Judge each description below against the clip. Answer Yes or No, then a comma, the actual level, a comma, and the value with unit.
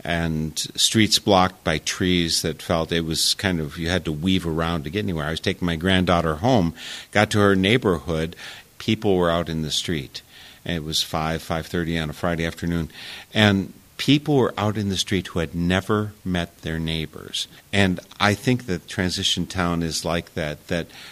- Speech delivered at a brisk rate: No, average, 195 wpm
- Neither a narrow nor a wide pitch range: Yes, average, 3.2 semitones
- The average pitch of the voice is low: Yes, very low, 85 Hz